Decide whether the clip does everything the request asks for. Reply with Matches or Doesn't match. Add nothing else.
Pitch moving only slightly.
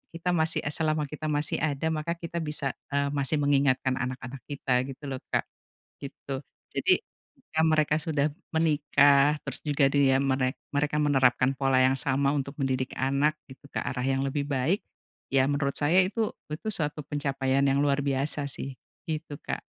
Matches